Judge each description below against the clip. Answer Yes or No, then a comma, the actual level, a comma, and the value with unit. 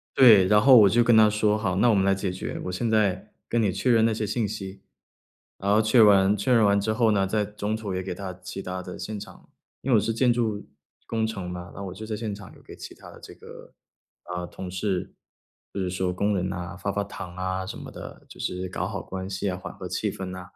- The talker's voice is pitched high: No, low, 100 Hz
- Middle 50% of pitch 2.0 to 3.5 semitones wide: Yes, average, 2.7 semitones